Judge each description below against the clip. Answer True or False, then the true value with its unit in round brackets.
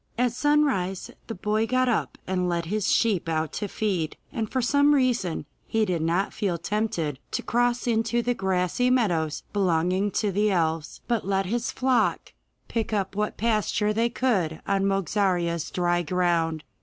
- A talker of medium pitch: False (200 Hz)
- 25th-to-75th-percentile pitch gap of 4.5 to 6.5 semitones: True (4.8 semitones)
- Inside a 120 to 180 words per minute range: True (165 wpm)